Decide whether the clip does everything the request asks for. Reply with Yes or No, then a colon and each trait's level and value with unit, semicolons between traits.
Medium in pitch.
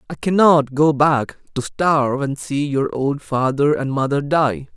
Yes: medium, 145 Hz